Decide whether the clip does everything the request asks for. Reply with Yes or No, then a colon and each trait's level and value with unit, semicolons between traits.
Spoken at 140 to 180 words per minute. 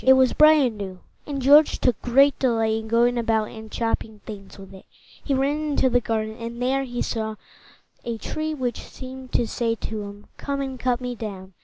No: fast, 205 wpm